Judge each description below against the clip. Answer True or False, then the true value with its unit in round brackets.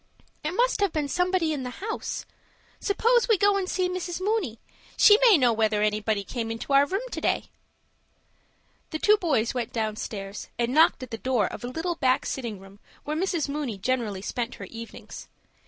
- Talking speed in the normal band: True (190 wpm)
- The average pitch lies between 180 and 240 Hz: False (275 Hz)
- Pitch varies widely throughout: True (8.3 semitones)